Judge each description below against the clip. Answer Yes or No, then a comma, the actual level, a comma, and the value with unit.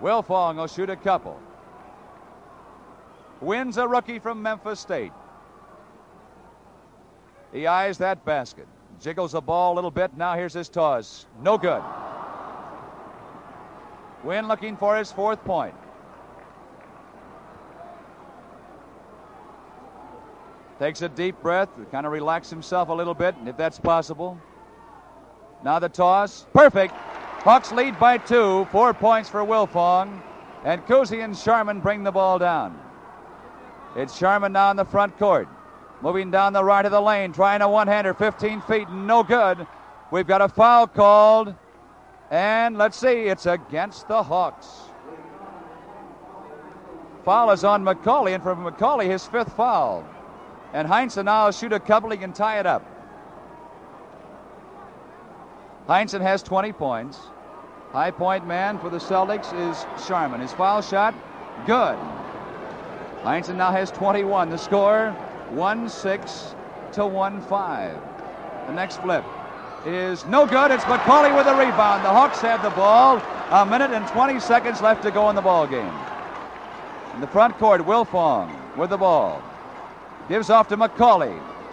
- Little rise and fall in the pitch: No, average, 3.2 semitones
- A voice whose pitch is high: Yes, high, 200 Hz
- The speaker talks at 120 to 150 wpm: Yes, average, 140 wpm